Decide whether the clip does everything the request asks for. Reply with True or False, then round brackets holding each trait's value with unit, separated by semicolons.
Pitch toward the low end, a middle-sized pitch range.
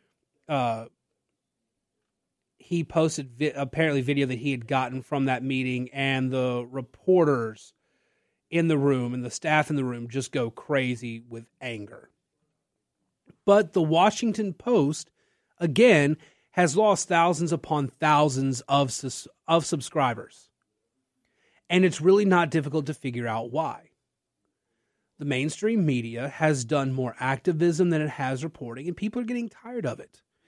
False (145 Hz; 4.6 semitones)